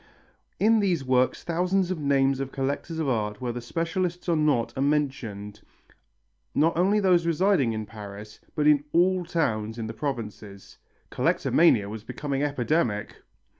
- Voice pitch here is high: No, medium, 140 Hz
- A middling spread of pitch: No, wide, 6.8 semitones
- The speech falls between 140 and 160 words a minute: Yes, average, 145 wpm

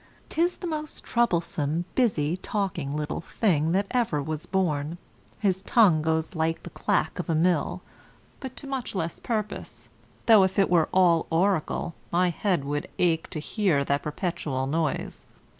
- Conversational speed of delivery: Yes, average, 160 wpm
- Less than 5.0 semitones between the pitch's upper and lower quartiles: Yes, average, 4.4 semitones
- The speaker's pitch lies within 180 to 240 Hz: No, medium, 170 Hz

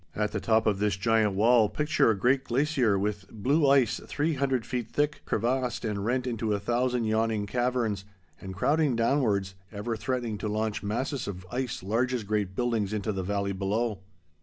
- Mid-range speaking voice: No, low, 115 Hz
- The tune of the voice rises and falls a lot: No, average, 3.6 semitones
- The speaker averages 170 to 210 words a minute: Yes, average, 185 wpm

